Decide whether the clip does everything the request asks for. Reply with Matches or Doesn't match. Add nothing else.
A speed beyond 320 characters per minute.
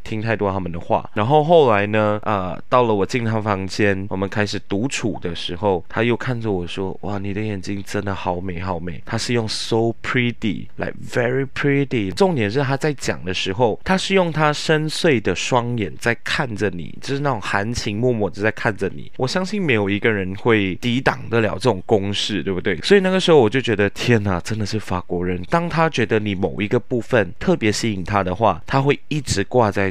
Matches